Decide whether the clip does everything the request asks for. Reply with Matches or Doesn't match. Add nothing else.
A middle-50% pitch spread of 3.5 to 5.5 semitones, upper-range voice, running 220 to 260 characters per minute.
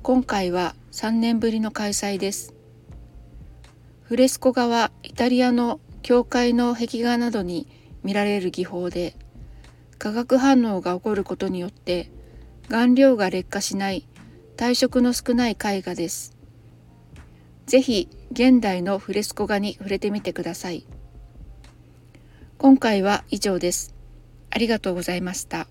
Matches